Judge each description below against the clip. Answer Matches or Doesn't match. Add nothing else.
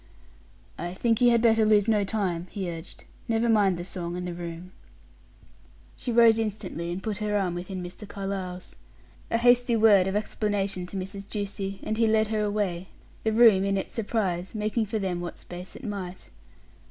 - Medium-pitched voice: Doesn't match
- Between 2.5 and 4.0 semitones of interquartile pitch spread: Matches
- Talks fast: Doesn't match